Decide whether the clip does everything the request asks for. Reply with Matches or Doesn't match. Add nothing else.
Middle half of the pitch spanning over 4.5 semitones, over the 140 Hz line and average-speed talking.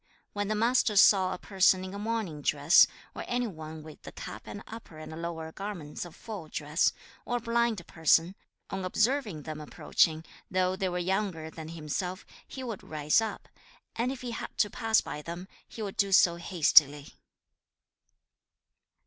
Matches